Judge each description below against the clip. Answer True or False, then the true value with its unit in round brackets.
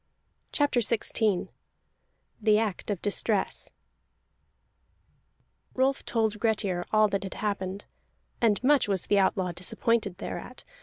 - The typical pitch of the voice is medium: False (210 Hz)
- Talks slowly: True (110 wpm)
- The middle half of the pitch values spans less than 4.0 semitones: True (2.7 semitones)